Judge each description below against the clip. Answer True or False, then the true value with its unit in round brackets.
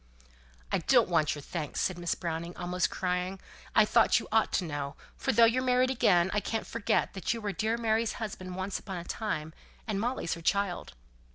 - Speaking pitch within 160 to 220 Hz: True (190 Hz)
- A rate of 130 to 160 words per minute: False (195 wpm)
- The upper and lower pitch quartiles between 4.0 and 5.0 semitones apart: True (4.4 semitones)